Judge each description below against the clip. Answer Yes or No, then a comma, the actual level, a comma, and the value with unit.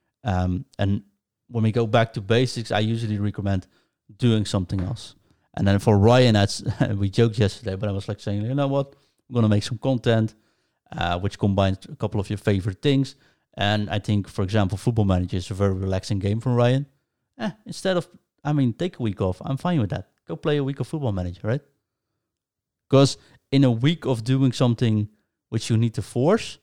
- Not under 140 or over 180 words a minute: No, fast, 205 wpm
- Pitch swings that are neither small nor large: Yes, average, 4.3 semitones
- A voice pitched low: Yes, low, 110 Hz